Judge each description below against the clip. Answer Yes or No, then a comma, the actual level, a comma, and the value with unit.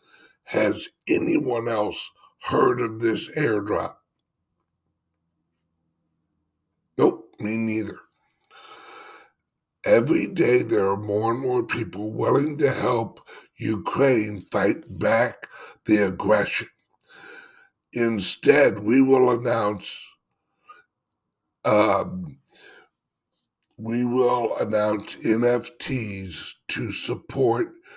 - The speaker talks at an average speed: No, slow, 80 wpm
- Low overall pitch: Yes, low, 120 Hz